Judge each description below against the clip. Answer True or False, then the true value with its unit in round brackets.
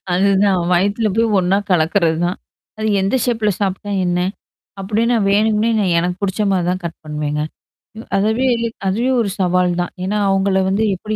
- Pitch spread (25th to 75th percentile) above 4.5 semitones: False (3.0 semitones)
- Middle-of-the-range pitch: False (195 Hz)